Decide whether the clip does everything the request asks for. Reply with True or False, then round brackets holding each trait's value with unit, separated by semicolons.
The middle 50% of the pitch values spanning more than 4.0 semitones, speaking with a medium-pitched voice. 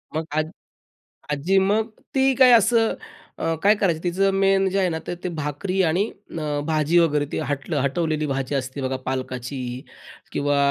True (5.2 semitones; 160 Hz)